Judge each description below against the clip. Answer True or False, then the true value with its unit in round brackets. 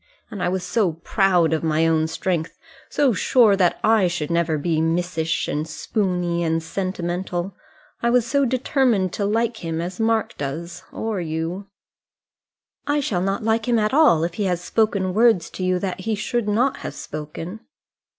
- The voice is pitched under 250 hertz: True (185 Hz)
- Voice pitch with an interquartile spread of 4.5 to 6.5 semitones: True (4.8 semitones)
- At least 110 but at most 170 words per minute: False (180 wpm)